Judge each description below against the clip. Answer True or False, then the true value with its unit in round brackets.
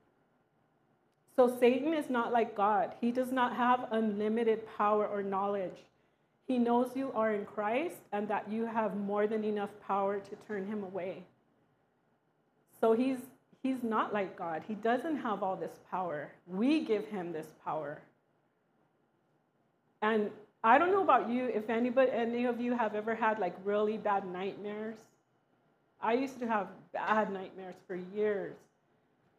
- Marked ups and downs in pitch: False (2.9 semitones)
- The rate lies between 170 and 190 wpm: False (155 wpm)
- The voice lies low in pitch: False (215 Hz)